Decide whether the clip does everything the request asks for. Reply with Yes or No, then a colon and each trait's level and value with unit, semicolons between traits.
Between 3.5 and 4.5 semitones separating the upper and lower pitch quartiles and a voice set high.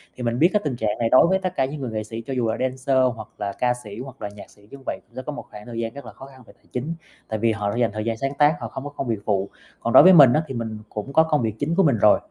No: average, 3.9 semitones; low, 125 Hz